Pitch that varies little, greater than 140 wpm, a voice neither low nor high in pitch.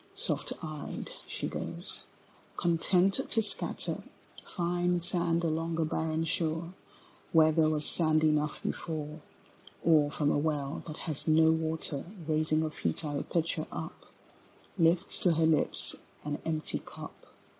No: narrow, 1.4 semitones; slow, 135 wpm; medium, 160 Hz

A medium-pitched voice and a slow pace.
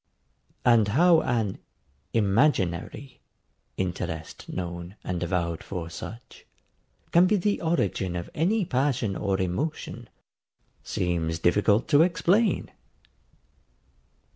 No: low, 105 Hz; slow, 95 wpm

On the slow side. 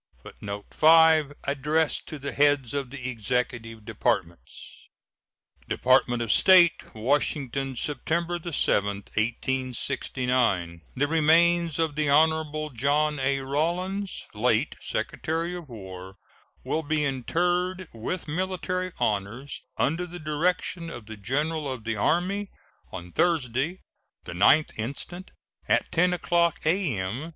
Yes: slow, 115 wpm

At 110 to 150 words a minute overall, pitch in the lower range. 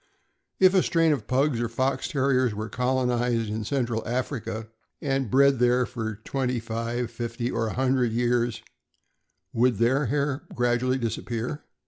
Yes: average, 145 wpm; low, 125 Hz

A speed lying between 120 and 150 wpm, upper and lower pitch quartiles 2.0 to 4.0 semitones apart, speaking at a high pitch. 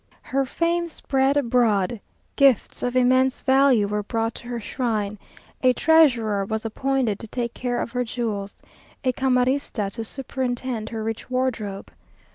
Yes: average, 145 wpm; average, 3.2 semitones; high, 245 Hz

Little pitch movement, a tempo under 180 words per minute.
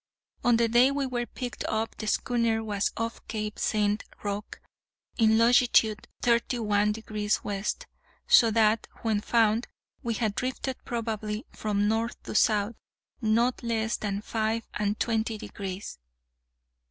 Yes: narrow, 1.9 semitones; average, 140 wpm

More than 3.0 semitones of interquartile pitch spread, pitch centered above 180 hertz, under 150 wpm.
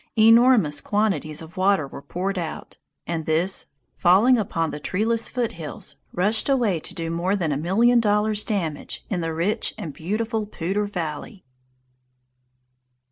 Yes: average, 4.8 semitones; high, 190 Hz; average, 140 wpm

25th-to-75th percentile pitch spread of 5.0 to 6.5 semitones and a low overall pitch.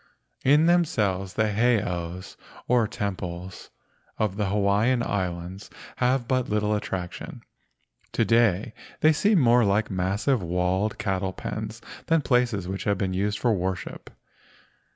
No: average, 4.2 semitones; low, 105 Hz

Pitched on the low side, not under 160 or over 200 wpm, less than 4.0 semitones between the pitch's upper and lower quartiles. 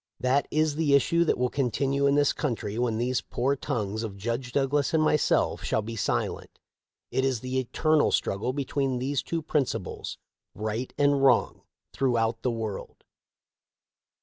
Yes: low, 130 Hz; average, 165 wpm; average, 3.5 semitones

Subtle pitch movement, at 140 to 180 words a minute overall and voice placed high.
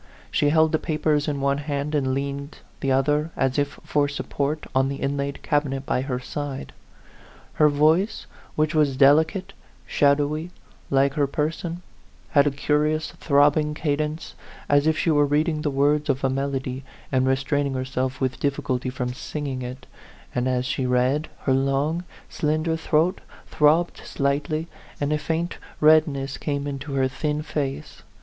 No: narrow, 2.0 semitones; average, 155 wpm; medium, 145 Hz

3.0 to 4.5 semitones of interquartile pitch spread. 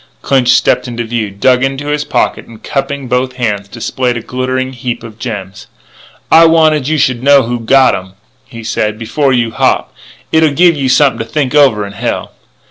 Yes: average, 3.5 semitones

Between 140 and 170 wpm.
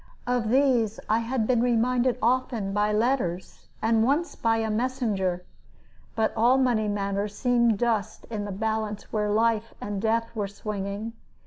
Yes: average, 150 wpm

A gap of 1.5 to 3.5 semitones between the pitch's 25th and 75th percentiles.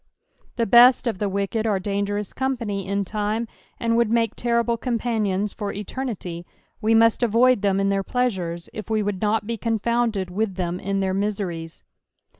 Yes: average, 2.9 semitones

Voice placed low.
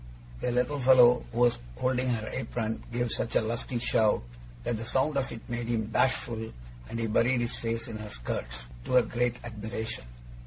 Yes: low, 120 Hz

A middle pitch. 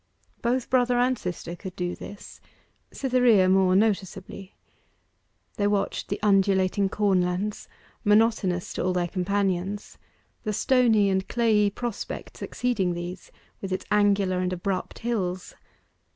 No: high, 200 Hz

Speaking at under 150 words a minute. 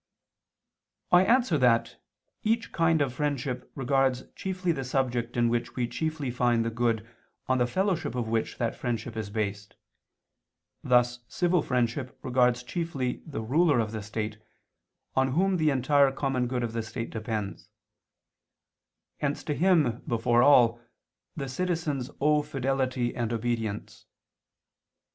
Yes: average, 140 wpm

